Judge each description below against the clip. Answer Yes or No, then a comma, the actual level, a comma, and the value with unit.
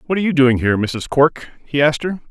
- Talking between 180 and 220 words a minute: No, fast, 260 wpm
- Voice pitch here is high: No, medium, 145 Hz